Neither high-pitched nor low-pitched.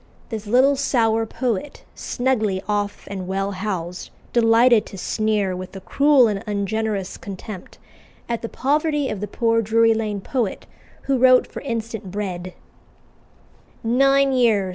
No: high, 220 Hz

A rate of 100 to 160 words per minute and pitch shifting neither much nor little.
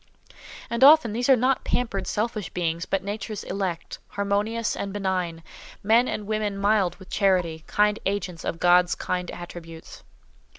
Yes: average, 145 wpm; average, 3.3 semitones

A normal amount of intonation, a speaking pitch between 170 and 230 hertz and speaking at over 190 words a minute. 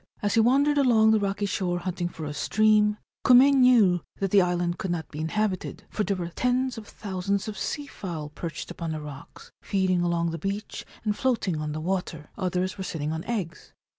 Yes: average, 4.1 semitones; high, 190 Hz; average, 200 wpm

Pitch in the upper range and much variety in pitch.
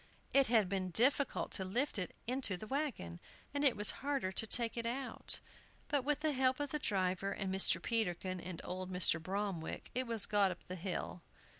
Yes: high, 210 Hz; wide, 5.9 semitones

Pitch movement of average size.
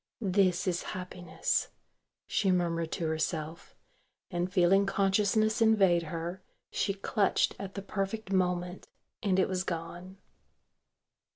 No: narrow, 2.2 semitones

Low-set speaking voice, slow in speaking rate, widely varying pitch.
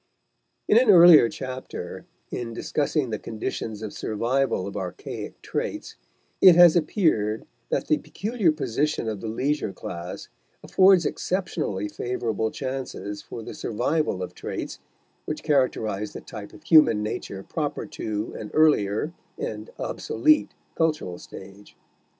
Yes: low, 125 Hz; slow, 130 wpm; wide, 6.7 semitones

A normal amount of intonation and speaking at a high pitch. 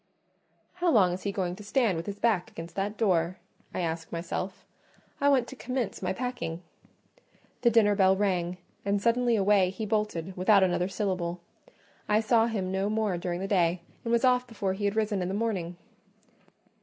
Yes: average, 3.6 semitones; high, 200 Hz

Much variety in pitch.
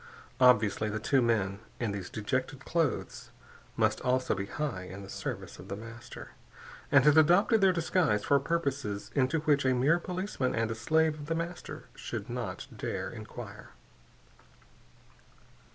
Yes: wide, 6.6 semitones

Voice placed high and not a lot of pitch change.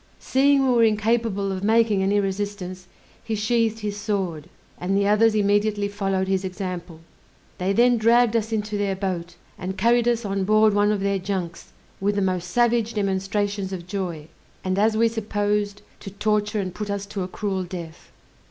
Yes: high, 205 Hz; narrow, 2.2 semitones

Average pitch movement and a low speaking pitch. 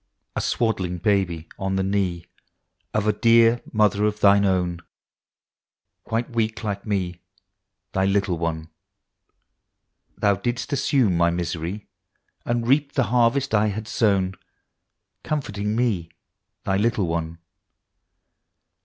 Yes: average, 4.1 semitones; low, 100 Hz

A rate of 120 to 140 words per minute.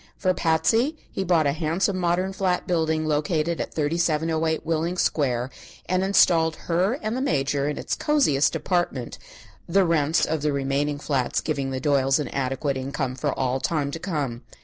No: average, 170 wpm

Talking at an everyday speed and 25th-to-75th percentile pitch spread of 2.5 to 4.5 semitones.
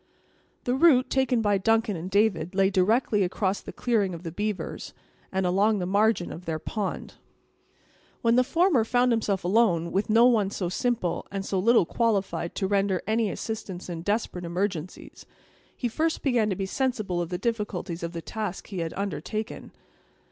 Yes: average, 170 wpm; average, 3.9 semitones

